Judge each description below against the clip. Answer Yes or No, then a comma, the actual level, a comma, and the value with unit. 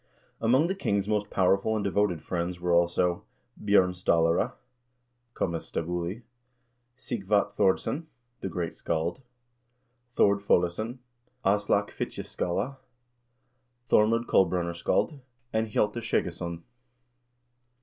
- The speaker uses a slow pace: Yes, slow, 95 wpm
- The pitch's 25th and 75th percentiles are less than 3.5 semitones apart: No, average, 3.8 semitones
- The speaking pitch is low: Yes, very low, 95 Hz